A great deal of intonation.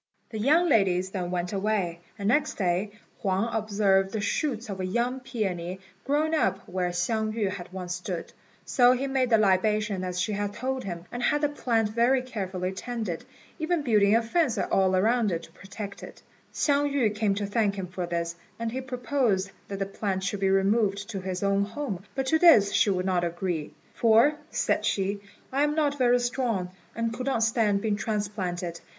No: average, 4.4 semitones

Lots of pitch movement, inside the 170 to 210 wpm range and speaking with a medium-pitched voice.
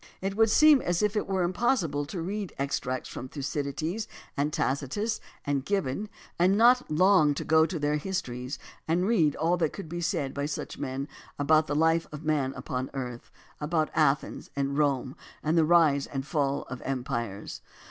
No: average, 4.3 semitones; average, 180 wpm; medium, 155 Hz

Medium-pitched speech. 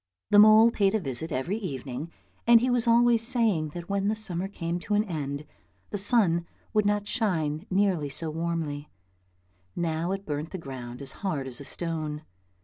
Yes: medium, 175 Hz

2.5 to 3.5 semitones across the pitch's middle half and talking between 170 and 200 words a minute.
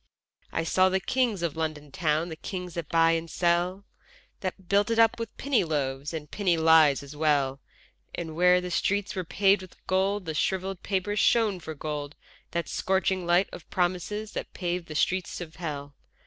Yes: average, 3.2 semitones; average, 185 wpm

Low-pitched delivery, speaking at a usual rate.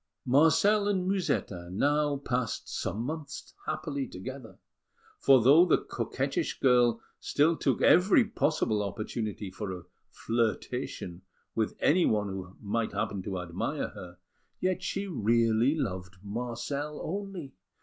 No: low, 125 Hz; slow, 120 wpm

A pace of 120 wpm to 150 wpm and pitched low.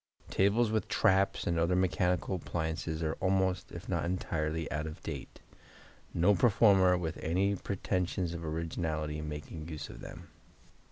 Yes: average, 145 wpm; very low, 85 Hz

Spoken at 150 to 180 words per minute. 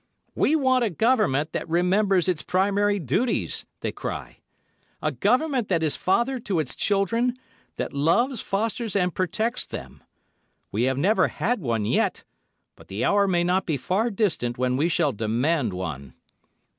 Yes: average, 155 wpm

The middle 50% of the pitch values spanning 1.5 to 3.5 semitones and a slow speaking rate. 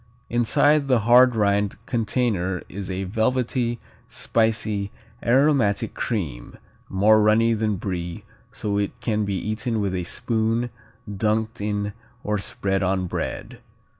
Yes: average, 2.8 semitones; slow, 125 wpm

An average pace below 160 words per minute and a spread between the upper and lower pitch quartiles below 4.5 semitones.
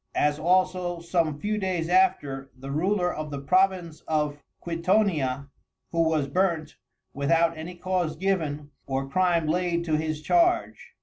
Yes: average, 140 wpm; average, 3.4 semitones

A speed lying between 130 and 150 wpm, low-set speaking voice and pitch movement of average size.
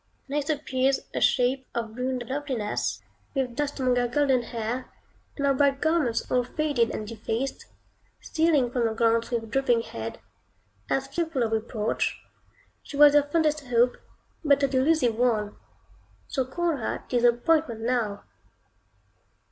No: average, 140 wpm; very high, 255 Hz; average, 3.5 semitones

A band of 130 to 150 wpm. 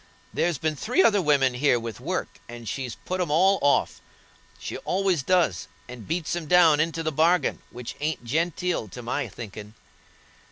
No: average, 170 wpm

